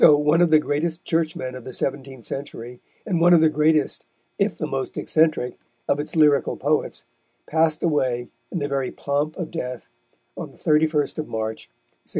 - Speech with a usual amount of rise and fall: Yes, average, 3.1 semitones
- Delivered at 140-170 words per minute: No, average, 180 wpm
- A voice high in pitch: No, medium, 150 Hz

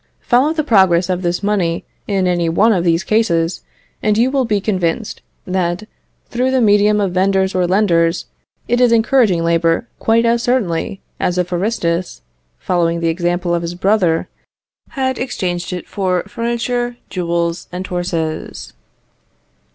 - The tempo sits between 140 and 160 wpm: Yes, average, 150 wpm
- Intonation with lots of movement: No, average, 4.6 semitones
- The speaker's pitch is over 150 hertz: Yes, medium, 185 Hz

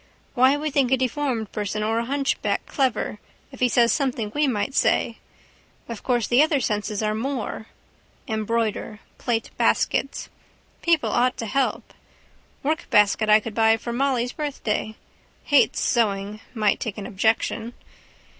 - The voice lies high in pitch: Yes, high, 235 Hz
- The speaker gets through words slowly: No, average, 145 wpm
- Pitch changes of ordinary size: Yes, average, 3.9 semitones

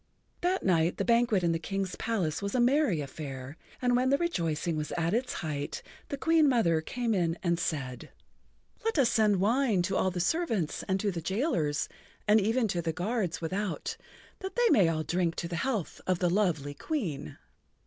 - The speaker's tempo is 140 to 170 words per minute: No, average, 195 wpm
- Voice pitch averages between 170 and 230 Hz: Yes, high, 190 Hz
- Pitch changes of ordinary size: No, wide, 6.5 semitones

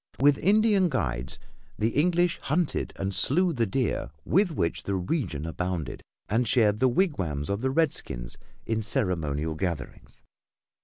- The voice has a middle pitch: No, low, 110 Hz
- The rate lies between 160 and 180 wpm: No, average, 140 wpm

